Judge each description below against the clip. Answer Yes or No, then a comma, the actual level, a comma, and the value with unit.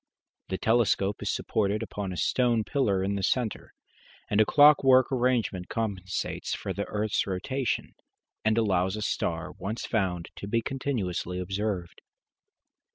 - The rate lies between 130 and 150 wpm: Yes, average, 140 wpm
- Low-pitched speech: Yes, low, 105 Hz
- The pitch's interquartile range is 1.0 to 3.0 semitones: No, average, 3.9 semitones